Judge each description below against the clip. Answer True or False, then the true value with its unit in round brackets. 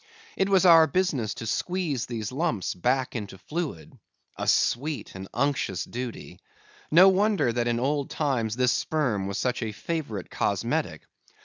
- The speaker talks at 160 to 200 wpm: False (150 wpm)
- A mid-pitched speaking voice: False (130 Hz)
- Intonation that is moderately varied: False (6.1 semitones)